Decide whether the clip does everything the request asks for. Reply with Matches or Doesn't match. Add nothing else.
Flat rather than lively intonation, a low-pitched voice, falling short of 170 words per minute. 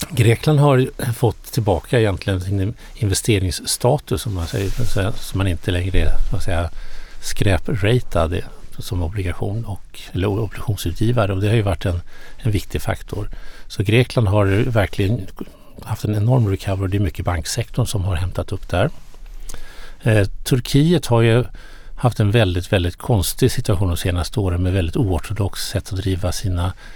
Doesn't match